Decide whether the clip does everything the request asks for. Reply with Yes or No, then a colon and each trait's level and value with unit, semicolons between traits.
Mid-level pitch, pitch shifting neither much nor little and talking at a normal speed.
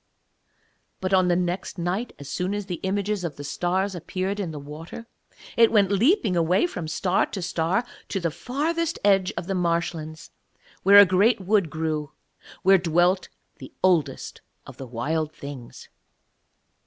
Yes: medium, 180 Hz; average, 3.6 semitones; average, 160 wpm